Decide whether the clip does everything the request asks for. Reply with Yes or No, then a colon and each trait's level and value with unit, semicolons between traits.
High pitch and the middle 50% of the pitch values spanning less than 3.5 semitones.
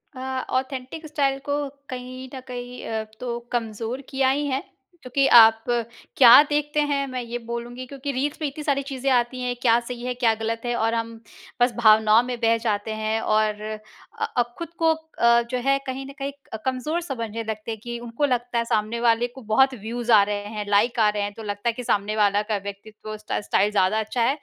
Yes: high, 240 Hz; average, 3.1 semitones